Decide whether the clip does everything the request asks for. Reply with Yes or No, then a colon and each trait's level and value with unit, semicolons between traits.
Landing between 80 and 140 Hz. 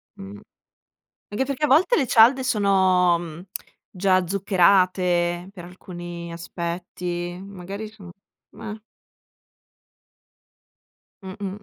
No: medium, 185 Hz